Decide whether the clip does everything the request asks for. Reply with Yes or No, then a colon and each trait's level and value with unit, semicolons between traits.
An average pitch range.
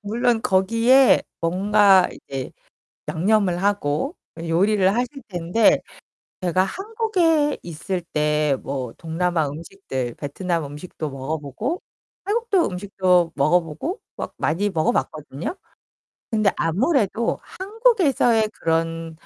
No: wide, 6.2 semitones